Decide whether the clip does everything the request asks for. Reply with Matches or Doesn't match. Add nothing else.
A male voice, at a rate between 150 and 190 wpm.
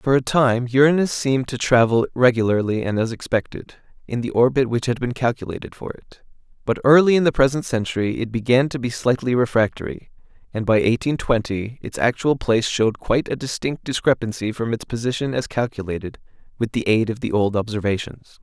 Matches